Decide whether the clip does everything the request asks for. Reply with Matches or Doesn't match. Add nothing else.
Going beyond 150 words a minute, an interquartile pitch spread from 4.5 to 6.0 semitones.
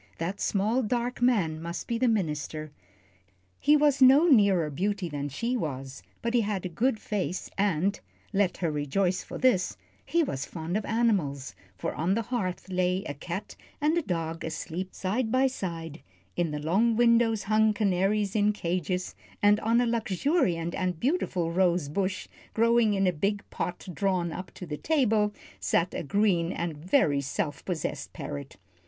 Matches